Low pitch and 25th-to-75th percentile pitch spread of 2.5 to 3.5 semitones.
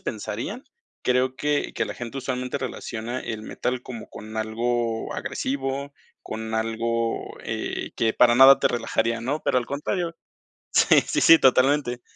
Yes: low, 125 Hz; average, 2.9 semitones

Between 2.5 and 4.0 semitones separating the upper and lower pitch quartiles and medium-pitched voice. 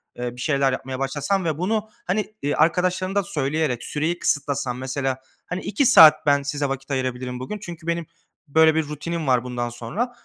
No: average, 4.6 semitones; medium, 145 Hz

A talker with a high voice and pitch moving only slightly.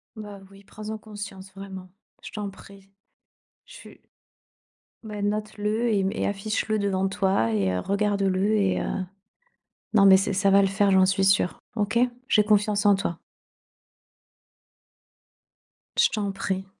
Yes: high, 200 Hz; narrow, 1.4 semitones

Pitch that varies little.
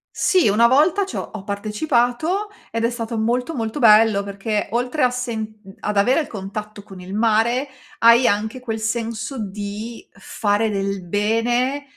No: average, 3.0 semitones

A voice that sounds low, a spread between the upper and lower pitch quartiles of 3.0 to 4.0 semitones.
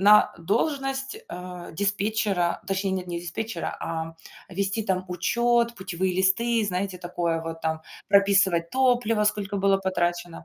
No: high, 190 Hz; average, 3.6 semitones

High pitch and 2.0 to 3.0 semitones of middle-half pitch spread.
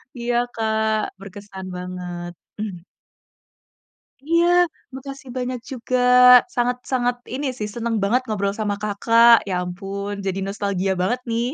No: high, 215 Hz; average, 3.7 semitones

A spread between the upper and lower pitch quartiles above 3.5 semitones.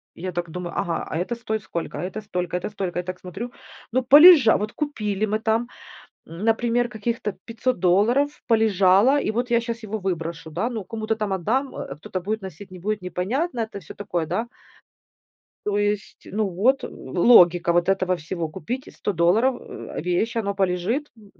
Yes: average, 4.3 semitones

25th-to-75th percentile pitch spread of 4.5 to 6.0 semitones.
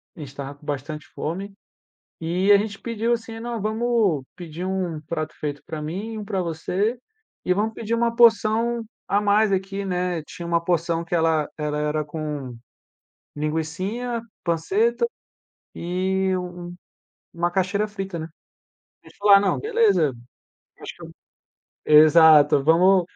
Yes: average, 4.9 semitones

